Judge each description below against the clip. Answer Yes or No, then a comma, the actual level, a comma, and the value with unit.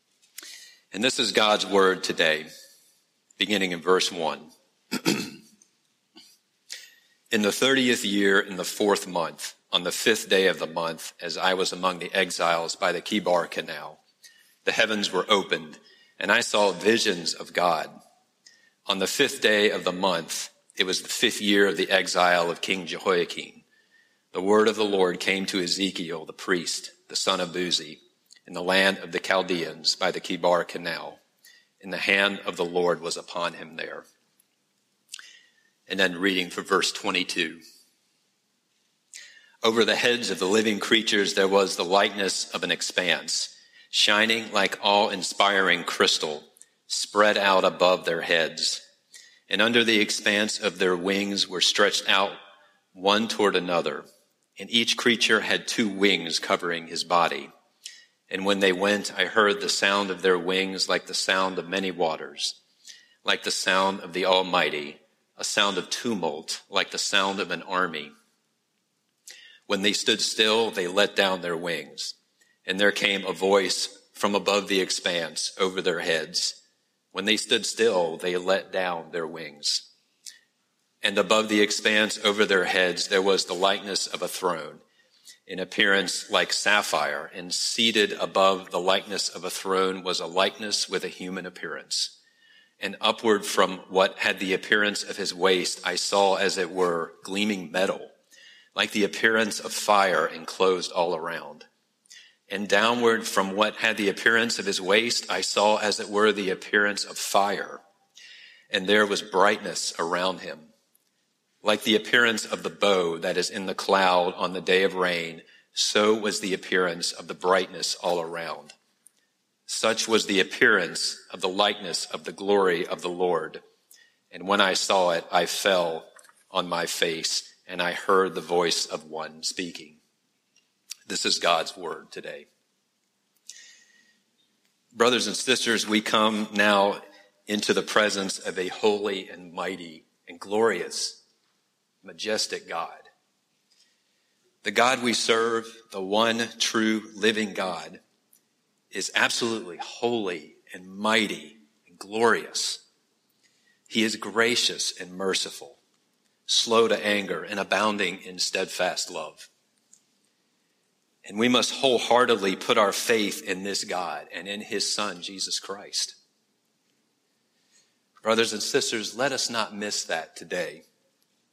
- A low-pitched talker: Yes, low, 100 Hz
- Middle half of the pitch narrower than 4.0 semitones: Yes, average, 2.8 semitones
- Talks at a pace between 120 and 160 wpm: Yes, average, 150 wpm